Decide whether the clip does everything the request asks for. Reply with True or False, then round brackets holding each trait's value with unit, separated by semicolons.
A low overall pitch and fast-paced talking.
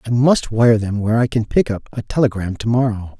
True (115 Hz; 245 wpm)